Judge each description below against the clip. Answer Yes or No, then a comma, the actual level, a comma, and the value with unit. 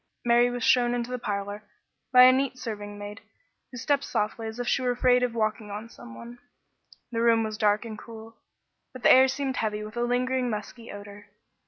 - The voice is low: No, high, 235 Hz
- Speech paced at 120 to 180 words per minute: No, average, 200 wpm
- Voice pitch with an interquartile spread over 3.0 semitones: No, average, 2.7 semitones